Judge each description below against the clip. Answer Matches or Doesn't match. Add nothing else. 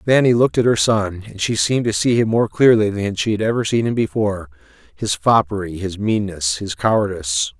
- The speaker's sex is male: Matches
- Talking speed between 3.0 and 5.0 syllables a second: Doesn't match